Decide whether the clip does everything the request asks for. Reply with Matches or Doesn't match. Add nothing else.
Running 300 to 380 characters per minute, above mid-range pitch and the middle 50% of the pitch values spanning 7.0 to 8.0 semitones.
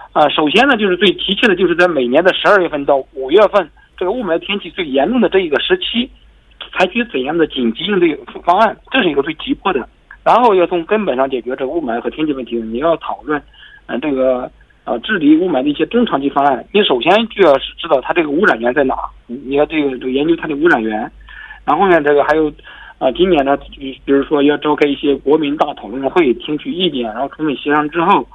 Doesn't match